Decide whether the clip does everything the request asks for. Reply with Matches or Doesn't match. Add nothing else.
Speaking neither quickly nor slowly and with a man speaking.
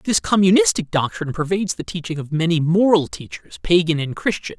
Matches